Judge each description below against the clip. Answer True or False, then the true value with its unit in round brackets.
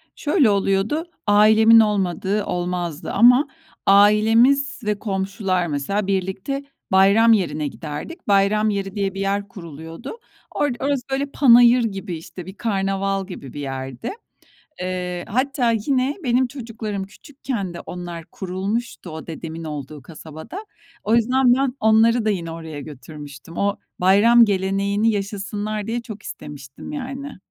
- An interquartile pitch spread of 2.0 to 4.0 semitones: False (4.5 semitones)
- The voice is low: False (200 Hz)